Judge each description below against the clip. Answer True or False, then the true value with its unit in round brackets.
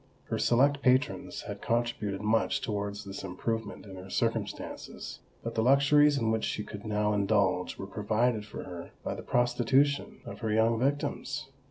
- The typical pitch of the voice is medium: False (110 Hz)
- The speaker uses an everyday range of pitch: True (4.0 semitones)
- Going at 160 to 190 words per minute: True (165 wpm)